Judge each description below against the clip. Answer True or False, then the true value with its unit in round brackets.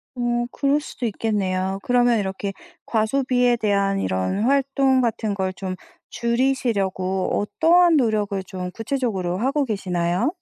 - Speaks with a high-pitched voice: True (220 Hz)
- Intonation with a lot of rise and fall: False (5.0 semitones)